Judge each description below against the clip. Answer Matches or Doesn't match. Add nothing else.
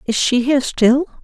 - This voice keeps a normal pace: Matches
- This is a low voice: Doesn't match